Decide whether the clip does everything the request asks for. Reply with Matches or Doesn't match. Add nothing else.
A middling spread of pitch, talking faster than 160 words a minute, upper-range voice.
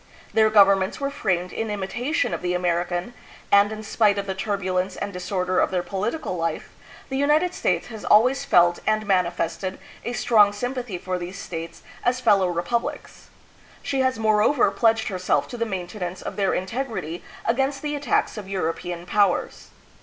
Matches